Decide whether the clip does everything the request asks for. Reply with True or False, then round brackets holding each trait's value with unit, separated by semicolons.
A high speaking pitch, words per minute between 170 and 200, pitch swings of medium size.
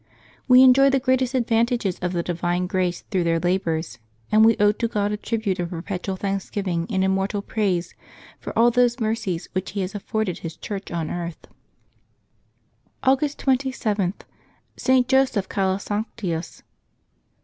False (200 Hz; 145 wpm; 4.6 semitones)